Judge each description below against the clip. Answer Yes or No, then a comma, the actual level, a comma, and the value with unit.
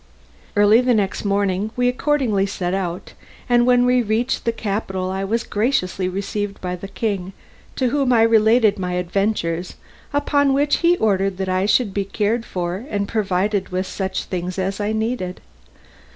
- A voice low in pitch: No, high, 205 Hz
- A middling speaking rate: Yes, average, 170 wpm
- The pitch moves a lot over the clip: No, average, 3.7 semitones